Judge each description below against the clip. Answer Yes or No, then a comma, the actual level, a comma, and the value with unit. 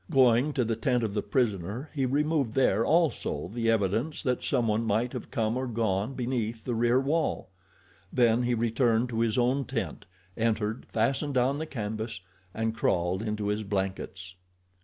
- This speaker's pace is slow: No, average, 165 wpm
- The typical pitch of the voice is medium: No, low, 115 Hz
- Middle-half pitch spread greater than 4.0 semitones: No, average, 3.1 semitones